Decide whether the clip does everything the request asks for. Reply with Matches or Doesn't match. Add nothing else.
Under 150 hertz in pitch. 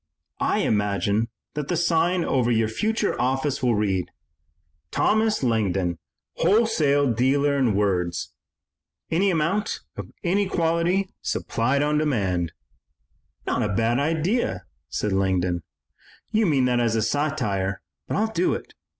Matches